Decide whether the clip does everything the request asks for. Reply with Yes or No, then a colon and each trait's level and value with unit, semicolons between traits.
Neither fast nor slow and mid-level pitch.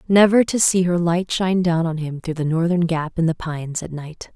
No: fast, 250 wpm; medium, 170 Hz